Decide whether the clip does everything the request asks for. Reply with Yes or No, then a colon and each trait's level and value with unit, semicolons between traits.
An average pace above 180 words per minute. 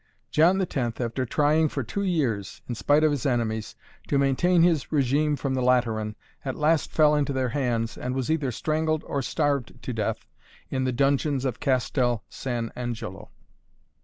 No: average, 170 wpm